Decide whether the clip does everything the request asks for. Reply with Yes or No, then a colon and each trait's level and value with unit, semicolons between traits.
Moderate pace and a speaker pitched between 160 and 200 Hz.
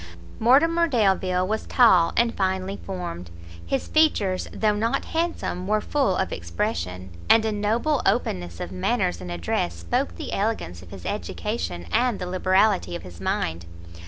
Yes: average, 155 wpm; medium, 185 Hz